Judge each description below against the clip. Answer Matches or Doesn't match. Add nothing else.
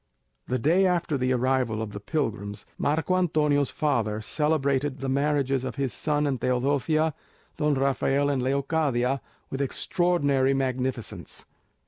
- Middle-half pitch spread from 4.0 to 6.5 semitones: Doesn't match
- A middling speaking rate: Doesn't match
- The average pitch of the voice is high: Doesn't match